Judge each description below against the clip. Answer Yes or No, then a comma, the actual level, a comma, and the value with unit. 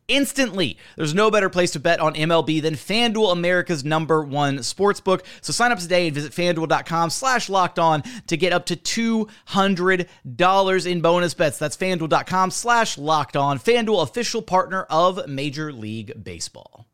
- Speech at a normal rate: Yes, average, 165 wpm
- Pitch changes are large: No, average, 3.8 semitones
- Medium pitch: Yes, medium, 175 Hz